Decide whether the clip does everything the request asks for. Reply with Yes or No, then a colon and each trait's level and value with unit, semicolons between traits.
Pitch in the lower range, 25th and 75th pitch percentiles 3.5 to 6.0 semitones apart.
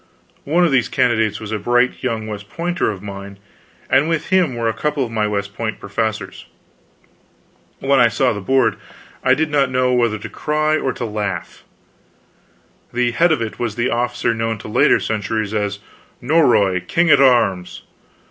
Yes: low, 120 Hz; average, 4.2 semitones